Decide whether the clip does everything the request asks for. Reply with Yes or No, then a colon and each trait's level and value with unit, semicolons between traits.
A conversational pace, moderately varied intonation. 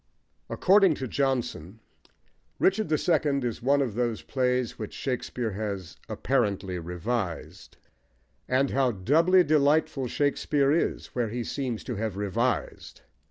No: slow, 125 wpm; average, 4.6 semitones